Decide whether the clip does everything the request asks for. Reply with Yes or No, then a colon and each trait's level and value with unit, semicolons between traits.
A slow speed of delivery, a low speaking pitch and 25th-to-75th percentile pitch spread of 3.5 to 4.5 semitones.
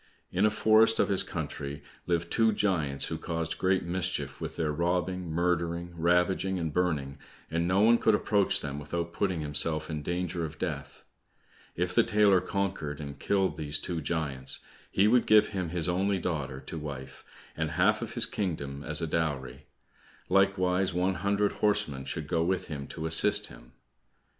No: average, 170 wpm; very low, 85 Hz; average, 3.8 semitones